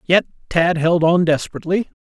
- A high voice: No, medium, 170 Hz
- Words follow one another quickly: No, average, 150 wpm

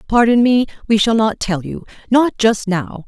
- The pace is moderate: Yes, average, 175 wpm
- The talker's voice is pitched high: Yes, high, 220 Hz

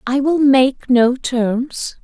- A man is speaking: No, female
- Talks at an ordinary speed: Yes, average, 150 wpm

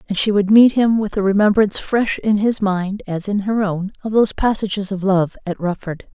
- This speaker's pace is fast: Yes, fast, 225 wpm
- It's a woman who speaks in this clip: Yes, female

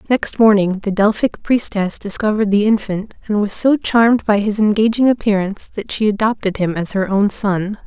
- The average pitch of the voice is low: No, high, 210 Hz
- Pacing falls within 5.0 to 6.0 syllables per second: Yes, 5.1 syllables/s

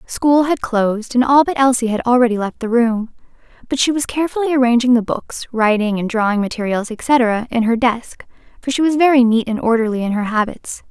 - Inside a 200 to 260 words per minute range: Yes, fast, 205 wpm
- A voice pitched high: Yes, high, 240 Hz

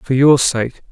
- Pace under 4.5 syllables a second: Yes, 4.0 syllables/s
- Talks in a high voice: No, low, 130 Hz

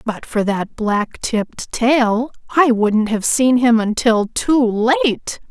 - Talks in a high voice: Yes, high, 230 Hz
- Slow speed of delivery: No, average, 155 wpm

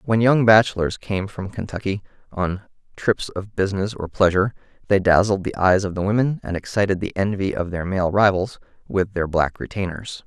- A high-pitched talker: No, low, 100 Hz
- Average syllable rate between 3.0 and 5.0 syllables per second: No, 5.3 syllables/s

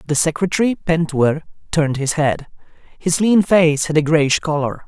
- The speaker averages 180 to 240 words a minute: No, average, 160 wpm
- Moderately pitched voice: Yes, medium, 160 Hz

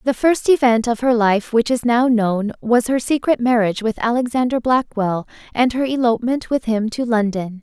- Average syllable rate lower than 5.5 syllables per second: Yes, 5.0 syllables/s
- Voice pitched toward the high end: Yes, high, 235 Hz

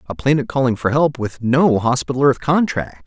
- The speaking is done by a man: Yes, male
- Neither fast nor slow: Yes, average, 195 wpm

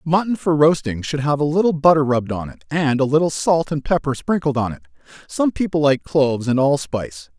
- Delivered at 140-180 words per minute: No, fast, 205 wpm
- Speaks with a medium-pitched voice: Yes, medium, 145 Hz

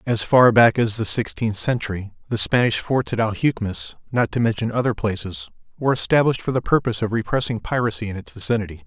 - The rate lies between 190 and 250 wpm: No, average, 175 wpm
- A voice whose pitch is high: No, low, 115 Hz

